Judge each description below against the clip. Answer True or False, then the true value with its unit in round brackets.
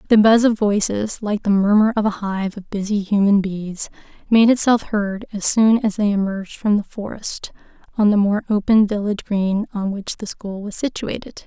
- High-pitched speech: True (205 Hz)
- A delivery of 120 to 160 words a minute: False (195 wpm)